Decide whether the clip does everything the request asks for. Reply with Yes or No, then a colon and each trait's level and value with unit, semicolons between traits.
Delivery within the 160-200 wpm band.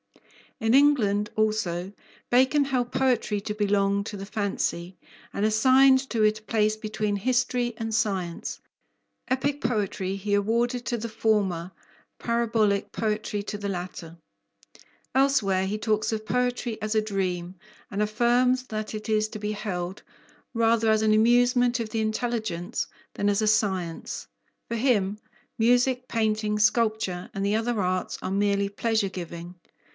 No: average, 145 wpm